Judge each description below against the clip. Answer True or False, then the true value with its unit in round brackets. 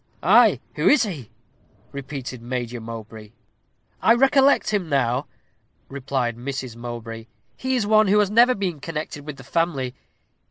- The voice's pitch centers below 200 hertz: True (140 Hz)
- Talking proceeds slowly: False (145 wpm)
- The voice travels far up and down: True (8.8 semitones)